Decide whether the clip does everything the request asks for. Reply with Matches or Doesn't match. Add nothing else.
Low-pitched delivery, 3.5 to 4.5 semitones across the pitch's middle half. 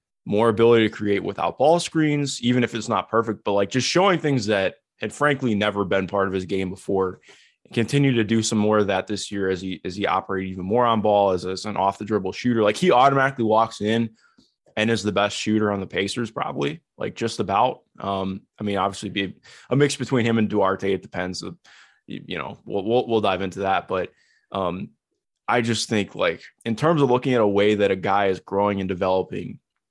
Doesn't match